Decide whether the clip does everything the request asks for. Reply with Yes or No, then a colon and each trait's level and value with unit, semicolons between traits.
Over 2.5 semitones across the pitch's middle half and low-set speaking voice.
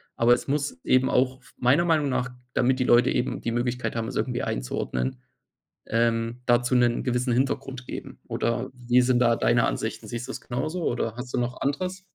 No: narrow, 1.7 semitones; low, 125 Hz